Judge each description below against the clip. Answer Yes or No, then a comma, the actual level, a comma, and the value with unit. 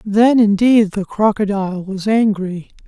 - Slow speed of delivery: Yes, slow, 125 wpm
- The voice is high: Yes, high, 205 Hz